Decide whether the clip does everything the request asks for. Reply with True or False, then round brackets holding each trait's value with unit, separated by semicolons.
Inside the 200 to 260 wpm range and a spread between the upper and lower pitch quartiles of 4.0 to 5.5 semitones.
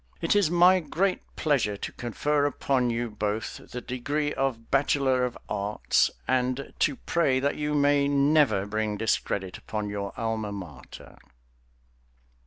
False (140 wpm; 5.2 semitones)